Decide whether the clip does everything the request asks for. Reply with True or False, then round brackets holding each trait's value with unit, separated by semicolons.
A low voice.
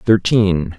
True (100 Hz)